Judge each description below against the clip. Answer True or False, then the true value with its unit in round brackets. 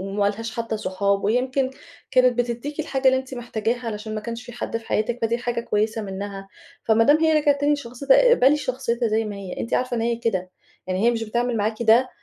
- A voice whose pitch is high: True (235 Hz)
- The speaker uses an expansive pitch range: False (3.0 semitones)